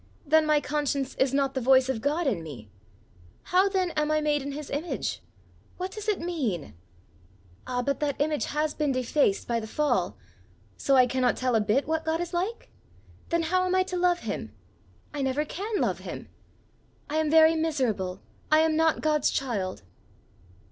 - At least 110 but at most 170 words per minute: No, average, 185 wpm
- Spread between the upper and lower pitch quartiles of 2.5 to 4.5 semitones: Yes, average, 3.8 semitones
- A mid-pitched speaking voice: No, very high, 295 Hz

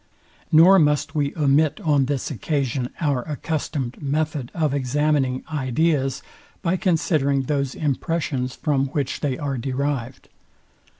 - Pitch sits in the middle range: Yes, medium, 145 Hz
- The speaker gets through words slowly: Yes, slow, 120 wpm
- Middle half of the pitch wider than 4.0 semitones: No, narrow, 2.5 semitones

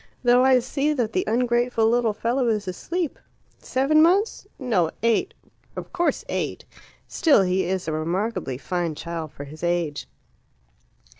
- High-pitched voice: Yes, high, 225 Hz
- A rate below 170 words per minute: Yes, average, 145 wpm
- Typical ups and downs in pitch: No, wide, 6.7 semitones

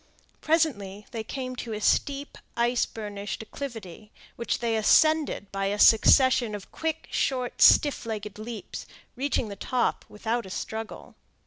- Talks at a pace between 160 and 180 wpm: No, average, 140 wpm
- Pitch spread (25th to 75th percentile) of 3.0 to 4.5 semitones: Yes, average, 3.8 semitones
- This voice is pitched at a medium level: No, high, 225 Hz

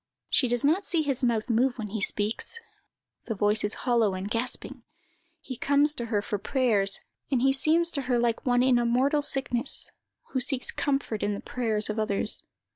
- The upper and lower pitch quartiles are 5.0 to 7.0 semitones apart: No, average, 3.8 semitones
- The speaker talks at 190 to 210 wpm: Yes, average, 195 wpm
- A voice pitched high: Yes, high, 245 Hz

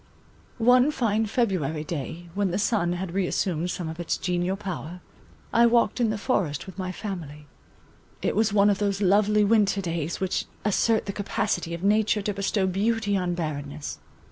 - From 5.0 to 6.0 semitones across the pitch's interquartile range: No, average, 3.4 semitones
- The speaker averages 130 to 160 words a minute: No, average, 170 wpm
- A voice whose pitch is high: Yes, high, 195 Hz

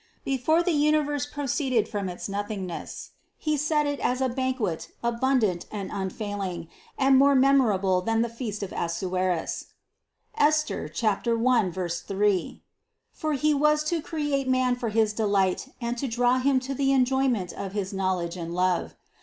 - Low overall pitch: No, high, 235 Hz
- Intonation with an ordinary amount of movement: No, wide, 6.1 semitones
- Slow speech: No, average, 155 wpm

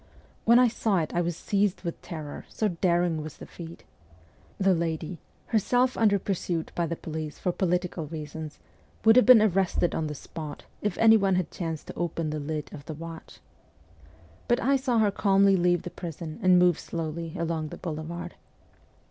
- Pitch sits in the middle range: Yes, medium, 175 Hz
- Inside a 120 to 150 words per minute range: No, average, 180 wpm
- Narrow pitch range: No, average, 3.7 semitones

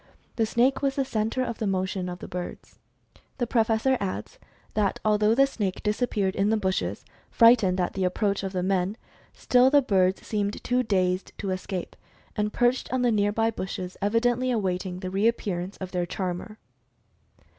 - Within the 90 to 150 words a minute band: No, average, 175 wpm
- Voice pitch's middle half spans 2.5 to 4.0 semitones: Yes, average, 3.7 semitones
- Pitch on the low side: No, high, 205 Hz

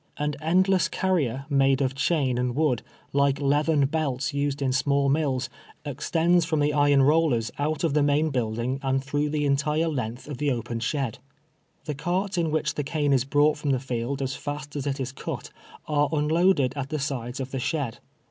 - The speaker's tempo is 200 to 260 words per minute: Yes, fast, 205 wpm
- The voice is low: No, medium, 145 Hz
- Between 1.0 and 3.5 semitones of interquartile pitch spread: Yes, narrow, 2.4 semitones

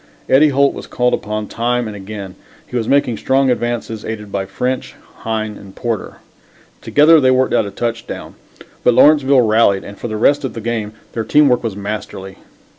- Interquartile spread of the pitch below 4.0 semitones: Yes, average, 3.5 semitones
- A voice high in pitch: No, low, 115 Hz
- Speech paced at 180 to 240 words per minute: Yes, average, 185 wpm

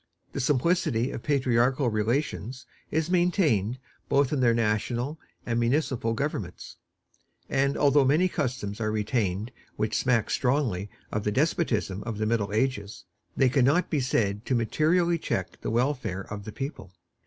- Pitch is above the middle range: No, low, 125 Hz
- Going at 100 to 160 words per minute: Yes, average, 150 wpm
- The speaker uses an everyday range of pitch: Yes, average, 4.8 semitones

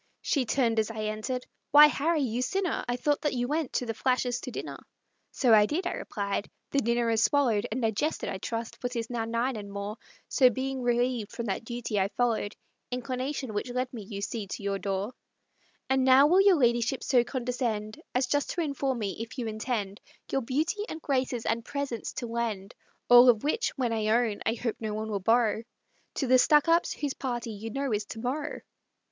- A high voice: Yes, high, 240 Hz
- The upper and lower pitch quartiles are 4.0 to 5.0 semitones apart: No, average, 3.3 semitones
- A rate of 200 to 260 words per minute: Yes, fast, 205 wpm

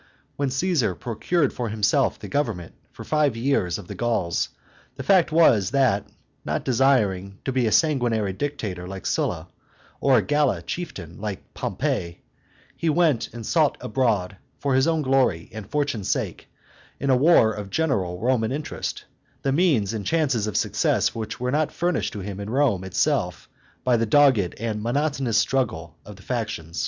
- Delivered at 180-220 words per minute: No, average, 165 wpm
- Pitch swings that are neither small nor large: No, wide, 5.8 semitones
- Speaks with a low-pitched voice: Yes, low, 120 Hz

